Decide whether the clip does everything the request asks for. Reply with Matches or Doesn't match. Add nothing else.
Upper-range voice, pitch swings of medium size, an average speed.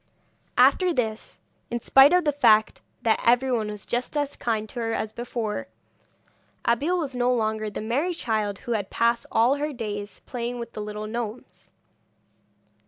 Matches